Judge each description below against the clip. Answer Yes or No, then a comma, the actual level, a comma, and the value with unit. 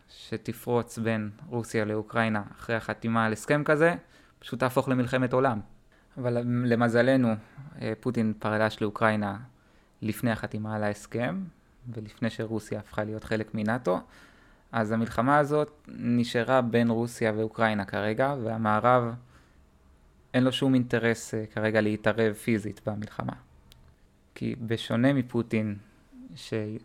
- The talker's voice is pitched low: Yes, low, 115 Hz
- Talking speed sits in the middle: Yes, average, 110 wpm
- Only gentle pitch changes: Yes, narrow, 2.3 semitones